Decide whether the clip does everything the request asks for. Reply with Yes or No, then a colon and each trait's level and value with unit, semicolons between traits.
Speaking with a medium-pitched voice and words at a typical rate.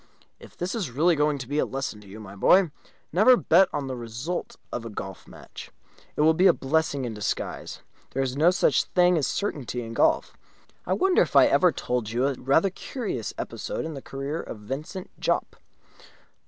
No: medium, 145 Hz; fast, 210 wpm